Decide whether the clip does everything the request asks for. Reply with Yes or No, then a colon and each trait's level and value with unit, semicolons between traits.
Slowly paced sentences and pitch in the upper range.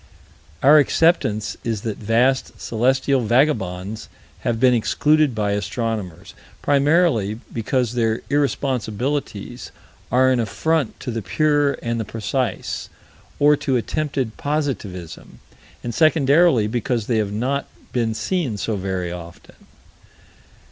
No: slow, 115 wpm; low, 120 Hz